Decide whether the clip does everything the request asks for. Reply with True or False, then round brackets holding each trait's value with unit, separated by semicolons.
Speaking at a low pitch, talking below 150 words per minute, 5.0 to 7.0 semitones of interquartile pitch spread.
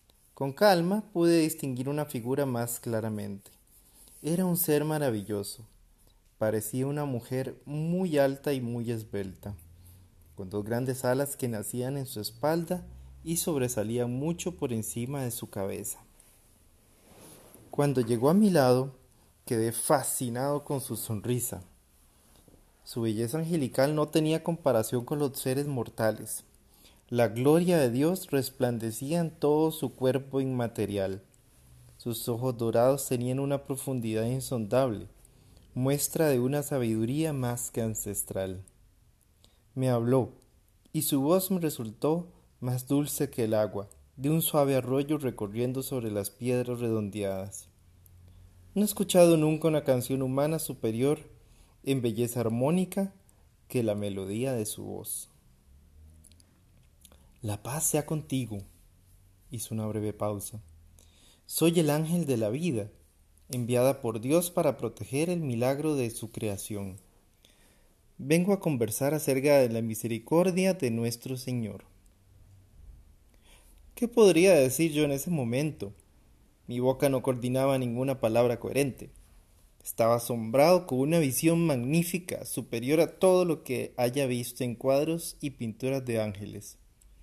True (125 Hz; 130 wpm; 5.5 semitones)